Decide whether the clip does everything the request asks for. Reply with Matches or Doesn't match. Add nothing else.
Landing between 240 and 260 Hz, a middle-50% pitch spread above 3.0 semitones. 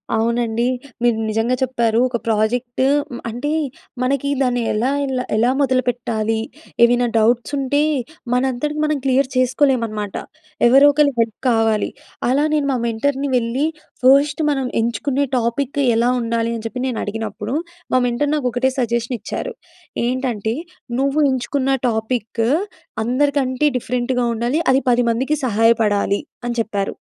Doesn't match